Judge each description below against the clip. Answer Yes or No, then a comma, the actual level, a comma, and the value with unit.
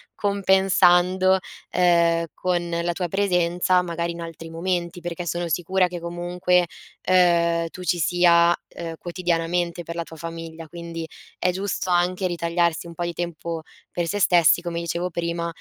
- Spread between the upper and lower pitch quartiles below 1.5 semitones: Yes, narrow, 1.1 semitones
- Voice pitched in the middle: Yes, medium, 175 Hz